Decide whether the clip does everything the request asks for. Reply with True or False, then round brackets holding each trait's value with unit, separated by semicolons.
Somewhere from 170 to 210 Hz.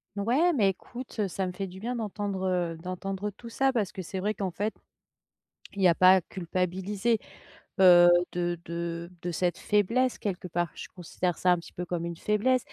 True (190 Hz)